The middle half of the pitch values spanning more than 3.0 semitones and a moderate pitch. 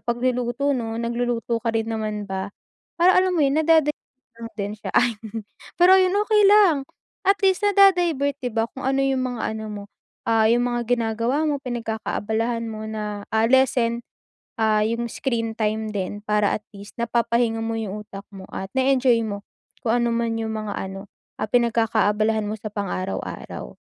No: average, 3.4 semitones; high, 230 Hz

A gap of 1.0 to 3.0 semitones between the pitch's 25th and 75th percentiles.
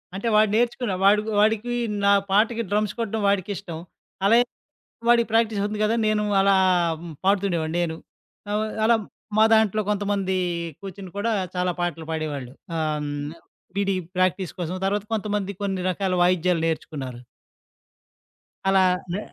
No: average, 3.4 semitones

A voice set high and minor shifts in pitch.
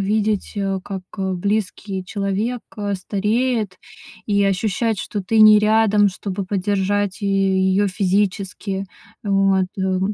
Yes: high, 200 Hz; narrow, 1.7 semitones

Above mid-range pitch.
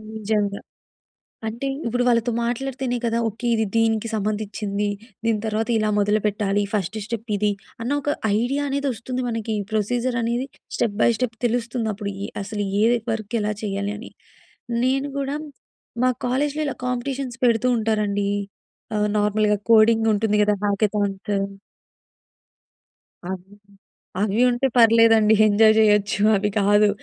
Yes: high, 220 Hz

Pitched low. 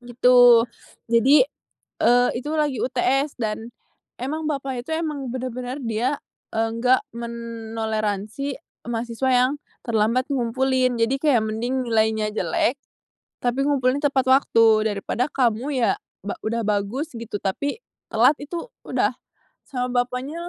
No: high, 245 Hz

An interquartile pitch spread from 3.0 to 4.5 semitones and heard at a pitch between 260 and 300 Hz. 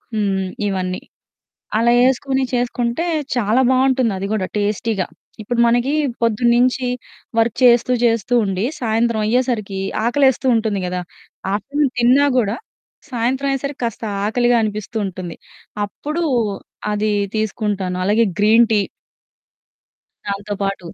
No: average, 3.3 semitones; high, 230 Hz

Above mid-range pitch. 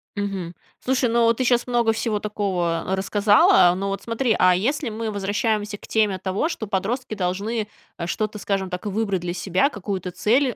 Yes: high, 205 Hz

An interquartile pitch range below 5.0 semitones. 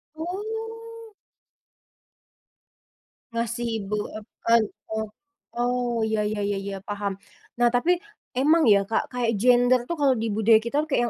No: wide, 5.4 semitones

